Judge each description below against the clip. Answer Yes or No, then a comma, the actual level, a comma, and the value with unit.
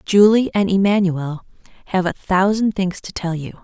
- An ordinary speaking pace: Yes, average, 165 wpm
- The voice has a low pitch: No, high, 190 Hz